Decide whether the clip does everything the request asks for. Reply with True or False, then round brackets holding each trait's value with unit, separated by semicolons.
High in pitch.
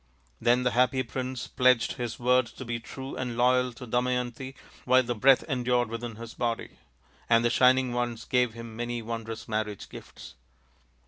False (120 Hz)